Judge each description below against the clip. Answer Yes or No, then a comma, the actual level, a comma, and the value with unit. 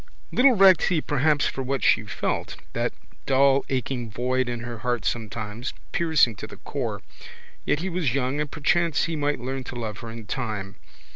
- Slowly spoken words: No, average, 185 wpm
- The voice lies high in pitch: No, low, 130 Hz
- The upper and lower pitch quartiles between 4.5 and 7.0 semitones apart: No, average, 4.1 semitones